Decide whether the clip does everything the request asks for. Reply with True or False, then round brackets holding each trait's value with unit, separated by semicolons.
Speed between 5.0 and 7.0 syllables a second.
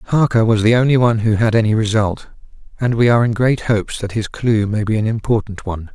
True (6.1 syllables/s)